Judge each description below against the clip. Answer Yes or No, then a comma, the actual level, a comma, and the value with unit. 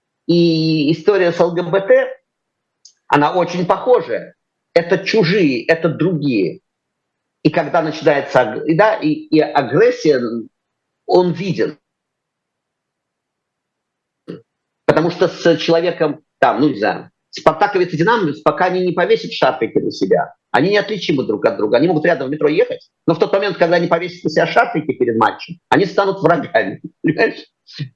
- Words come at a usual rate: Yes, average, 140 wpm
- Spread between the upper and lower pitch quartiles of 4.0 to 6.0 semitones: No, average, 3.6 semitones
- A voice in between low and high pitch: Yes, medium, 180 Hz